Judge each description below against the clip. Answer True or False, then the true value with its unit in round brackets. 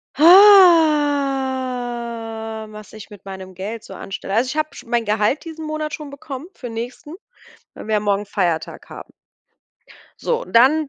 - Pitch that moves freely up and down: True (5.9 semitones)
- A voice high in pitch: True (245 Hz)